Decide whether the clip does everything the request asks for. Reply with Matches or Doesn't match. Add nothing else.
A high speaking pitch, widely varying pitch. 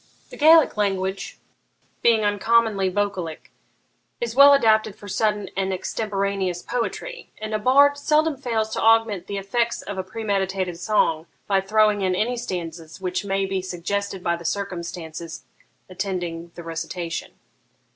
Doesn't match